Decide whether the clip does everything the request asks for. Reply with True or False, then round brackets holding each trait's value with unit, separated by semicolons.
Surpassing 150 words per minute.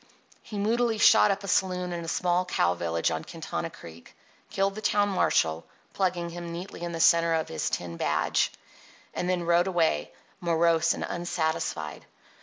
True (170 wpm)